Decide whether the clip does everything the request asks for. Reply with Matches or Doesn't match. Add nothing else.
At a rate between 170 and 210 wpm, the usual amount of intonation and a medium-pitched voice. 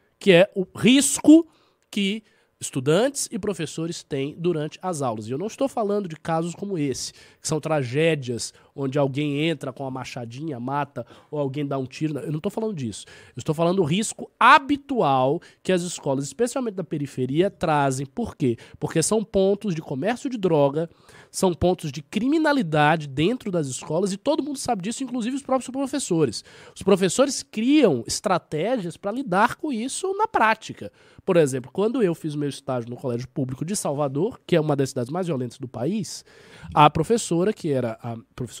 Doesn't match